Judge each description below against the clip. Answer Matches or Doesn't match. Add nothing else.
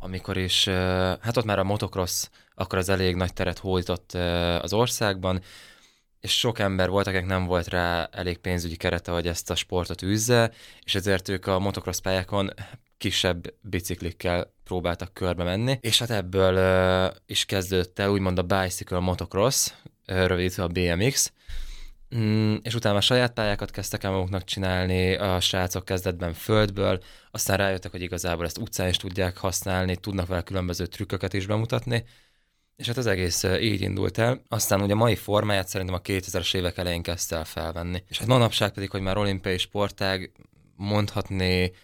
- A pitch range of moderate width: Doesn't match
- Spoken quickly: Matches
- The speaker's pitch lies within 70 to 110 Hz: Matches